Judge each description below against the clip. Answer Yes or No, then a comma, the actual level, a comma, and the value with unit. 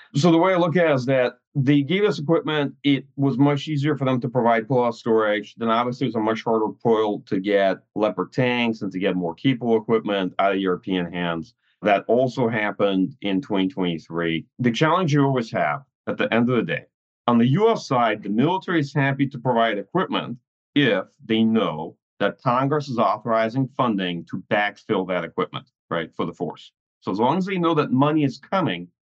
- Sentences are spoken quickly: Yes, fast, 205 wpm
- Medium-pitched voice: No, low, 120 Hz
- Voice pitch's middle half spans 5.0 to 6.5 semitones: Yes, wide, 5.5 semitones